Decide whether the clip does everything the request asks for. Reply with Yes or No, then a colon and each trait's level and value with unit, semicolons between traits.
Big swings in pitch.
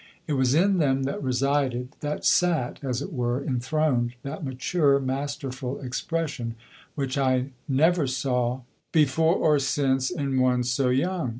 No: average, 2.8 semitones